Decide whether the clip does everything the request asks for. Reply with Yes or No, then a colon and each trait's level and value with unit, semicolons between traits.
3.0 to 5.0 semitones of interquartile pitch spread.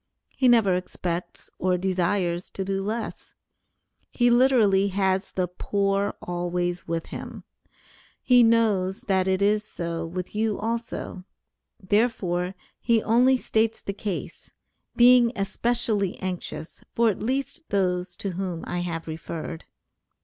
Yes: average, 3.9 semitones